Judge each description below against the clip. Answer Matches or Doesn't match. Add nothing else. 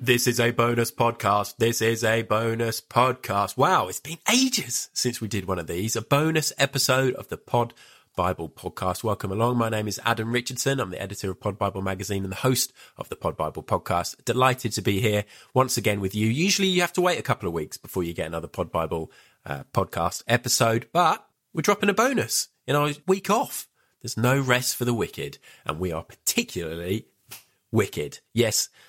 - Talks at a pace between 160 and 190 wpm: Doesn't match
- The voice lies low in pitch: Matches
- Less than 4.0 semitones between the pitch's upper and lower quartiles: Doesn't match